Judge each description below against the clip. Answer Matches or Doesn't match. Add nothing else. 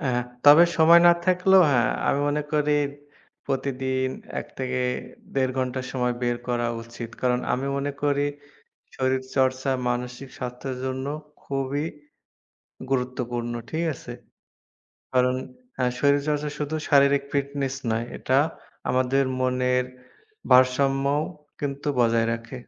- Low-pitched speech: Matches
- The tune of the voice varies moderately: Doesn't match